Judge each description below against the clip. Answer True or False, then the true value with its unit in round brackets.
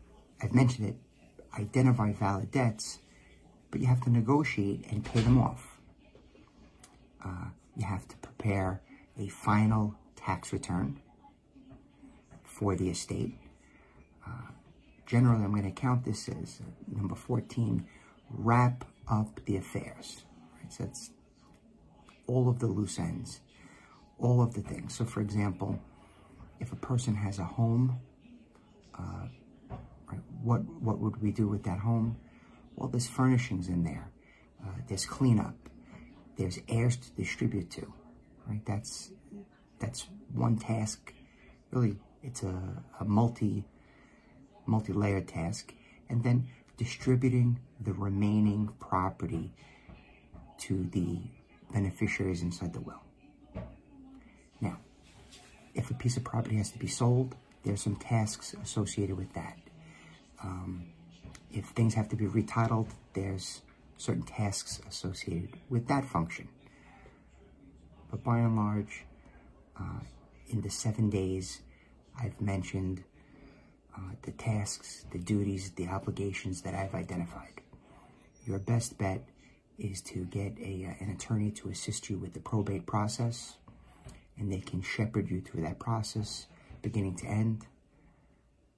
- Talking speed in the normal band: False (125 wpm)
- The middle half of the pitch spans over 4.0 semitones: False (3.7 semitones)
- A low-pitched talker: True (105 Hz)